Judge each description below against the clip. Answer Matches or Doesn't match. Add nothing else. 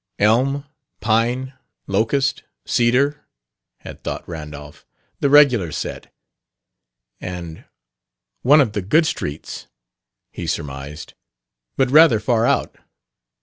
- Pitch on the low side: Matches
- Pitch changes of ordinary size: Doesn't match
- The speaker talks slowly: Matches